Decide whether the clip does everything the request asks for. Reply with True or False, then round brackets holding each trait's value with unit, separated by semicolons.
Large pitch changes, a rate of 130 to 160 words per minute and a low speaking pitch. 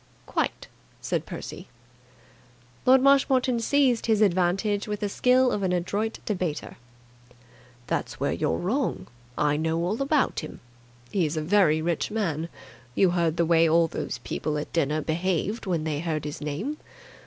False (5.7 semitones; 155 wpm; 180 Hz)